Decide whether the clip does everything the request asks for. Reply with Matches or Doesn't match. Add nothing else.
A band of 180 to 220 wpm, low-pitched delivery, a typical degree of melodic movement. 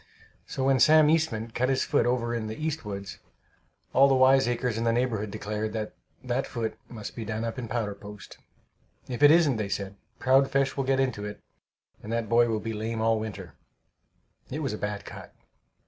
Matches